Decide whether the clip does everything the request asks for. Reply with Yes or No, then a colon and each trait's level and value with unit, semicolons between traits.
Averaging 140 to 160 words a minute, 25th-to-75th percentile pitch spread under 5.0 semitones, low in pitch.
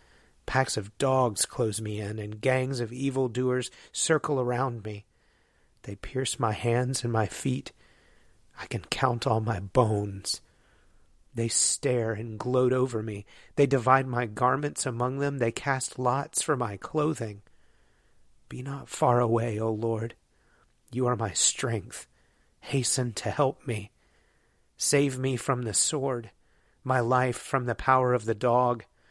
Yes: average, 150 wpm; average, 2.8 semitones; low, 125 Hz